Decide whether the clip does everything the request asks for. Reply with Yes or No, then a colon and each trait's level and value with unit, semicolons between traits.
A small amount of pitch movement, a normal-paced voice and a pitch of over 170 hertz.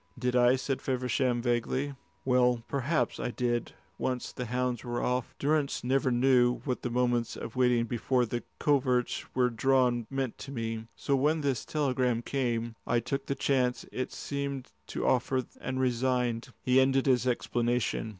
No: narrow, 1.7 semitones; average, 160 wpm; low, 125 Hz